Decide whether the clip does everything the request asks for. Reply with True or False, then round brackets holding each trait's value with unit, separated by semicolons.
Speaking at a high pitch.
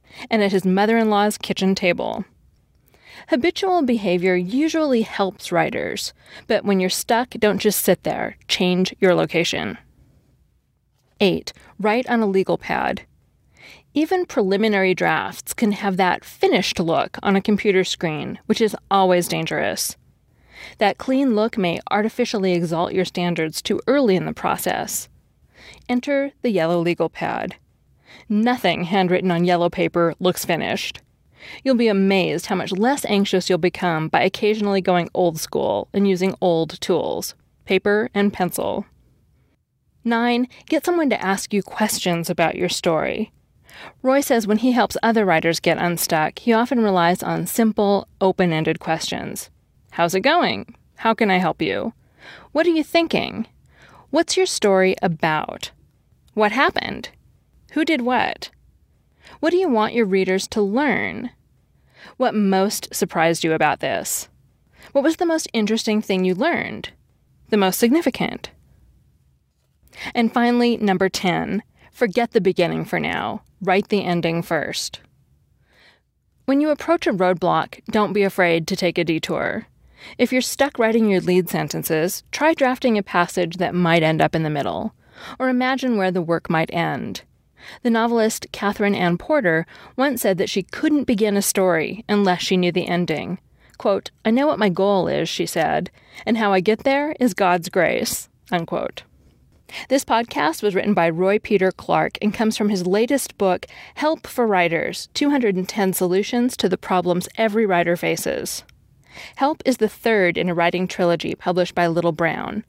True (200 Hz)